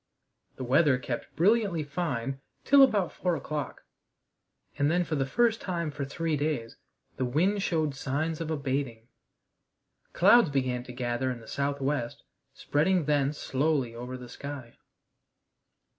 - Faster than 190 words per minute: No, average, 140 wpm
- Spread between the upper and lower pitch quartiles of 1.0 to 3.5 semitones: No, average, 4.3 semitones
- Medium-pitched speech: Yes, medium, 145 Hz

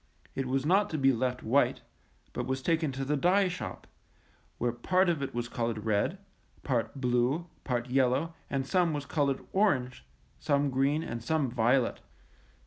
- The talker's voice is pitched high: No, low, 135 Hz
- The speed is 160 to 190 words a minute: Yes, average, 165 wpm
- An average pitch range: Yes, average, 4.3 semitones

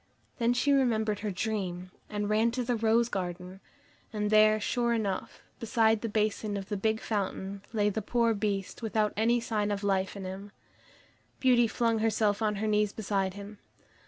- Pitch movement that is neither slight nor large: No, narrow, 2.0 semitones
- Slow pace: No, average, 175 wpm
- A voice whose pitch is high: Yes, high, 215 Hz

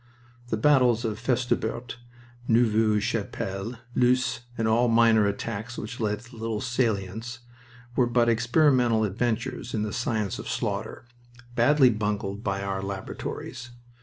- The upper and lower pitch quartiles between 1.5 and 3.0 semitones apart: Yes, narrow, 2.4 semitones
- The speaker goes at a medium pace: No, slow, 130 wpm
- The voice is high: No, low, 115 Hz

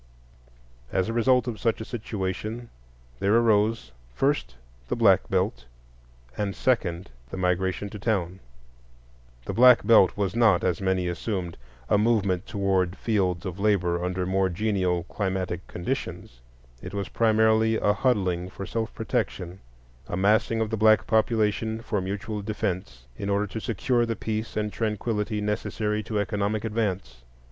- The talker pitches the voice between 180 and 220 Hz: No, low, 105 Hz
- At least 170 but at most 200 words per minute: No, average, 145 wpm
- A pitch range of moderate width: Yes, average, 3.2 semitones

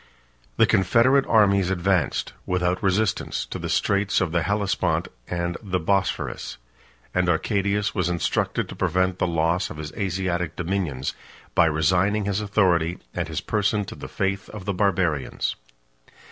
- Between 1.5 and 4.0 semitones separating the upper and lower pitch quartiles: Yes, narrow, 2.5 semitones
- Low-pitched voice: Yes, very low, 95 Hz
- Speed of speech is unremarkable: Yes, average, 145 wpm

